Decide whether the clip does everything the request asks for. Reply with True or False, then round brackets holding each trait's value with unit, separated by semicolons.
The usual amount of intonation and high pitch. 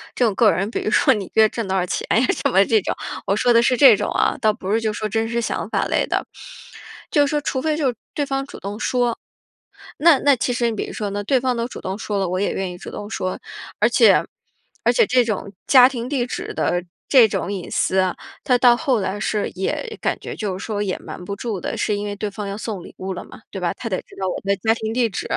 True (3.9 semitones; 215 Hz)